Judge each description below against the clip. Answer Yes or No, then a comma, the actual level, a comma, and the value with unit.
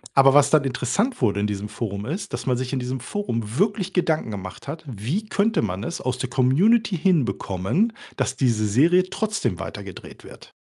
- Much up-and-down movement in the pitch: Yes, wide, 8.3 semitones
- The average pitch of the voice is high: No, low, 135 Hz